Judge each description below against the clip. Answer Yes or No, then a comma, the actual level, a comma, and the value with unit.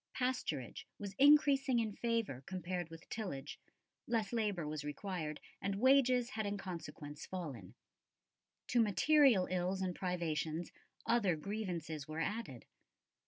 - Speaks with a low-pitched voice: No, high, 190 Hz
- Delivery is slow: Yes, slow, 120 wpm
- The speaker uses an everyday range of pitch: No, wide, 6.2 semitones